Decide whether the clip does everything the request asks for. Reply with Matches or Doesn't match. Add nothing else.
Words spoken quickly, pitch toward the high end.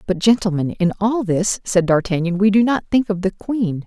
Matches